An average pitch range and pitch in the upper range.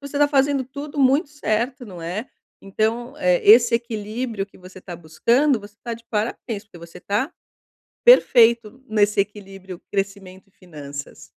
Yes: average, 4.7 semitones; high, 215 Hz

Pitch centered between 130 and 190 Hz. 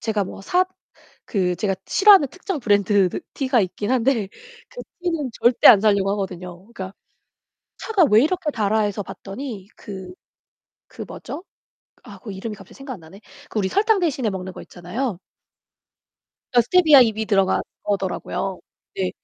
No: high, 215 Hz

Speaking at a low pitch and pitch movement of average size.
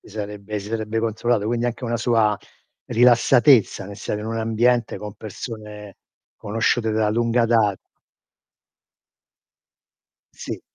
No: low, 110 Hz; narrow, 1.9 semitones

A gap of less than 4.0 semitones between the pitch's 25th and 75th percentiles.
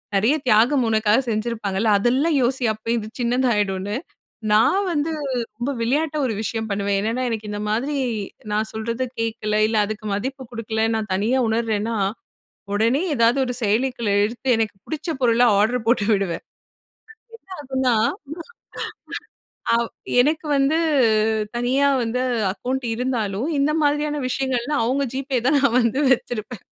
Yes: average, 3.5 semitones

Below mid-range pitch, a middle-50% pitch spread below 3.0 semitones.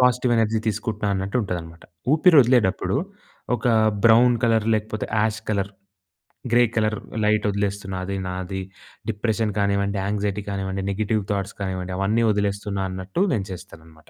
Yes: low, 100 Hz; narrow, 2.4 semitones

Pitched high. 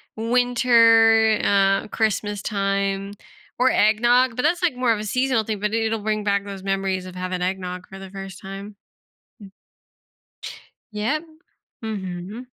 Yes: high, 210 Hz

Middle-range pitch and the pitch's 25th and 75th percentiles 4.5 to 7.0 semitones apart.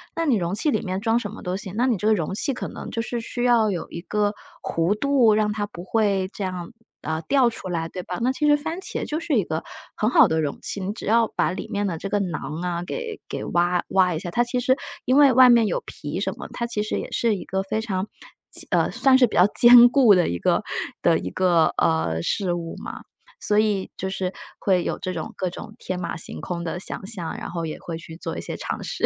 No: high, 200 Hz; average, 5.1 semitones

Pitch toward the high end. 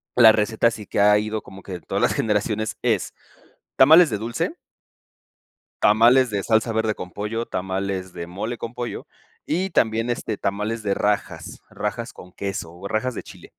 No: low, 110 Hz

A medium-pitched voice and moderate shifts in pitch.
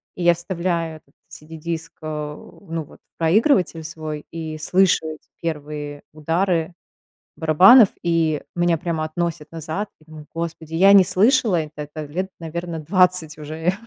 No: medium, 165 Hz; narrow, 2.1 semitones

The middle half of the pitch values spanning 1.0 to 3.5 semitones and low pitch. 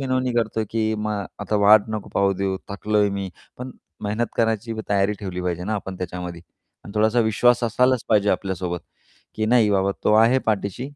Yes: narrow, 2.5 semitones; low, 105 Hz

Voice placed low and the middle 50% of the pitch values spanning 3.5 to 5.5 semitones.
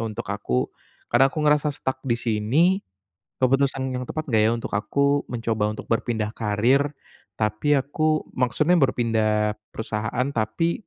Yes: low, 125 Hz; average, 4.4 semitones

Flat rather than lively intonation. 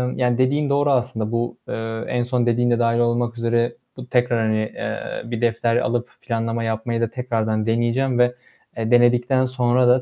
Yes: narrow, 1.1 semitones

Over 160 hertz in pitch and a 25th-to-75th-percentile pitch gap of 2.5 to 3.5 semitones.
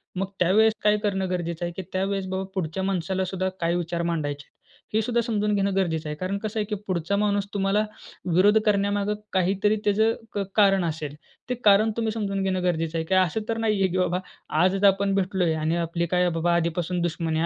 Yes: high, 190 Hz; average, 3.0 semitones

